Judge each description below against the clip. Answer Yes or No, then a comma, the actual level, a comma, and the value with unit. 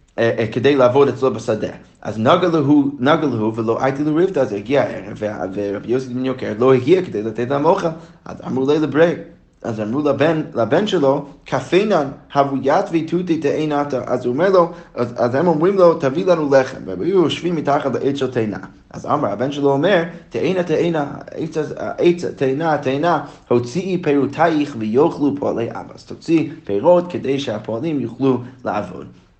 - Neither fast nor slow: No, fast, 160 wpm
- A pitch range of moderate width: Yes, average, 4.8 semitones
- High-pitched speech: No, medium, 140 Hz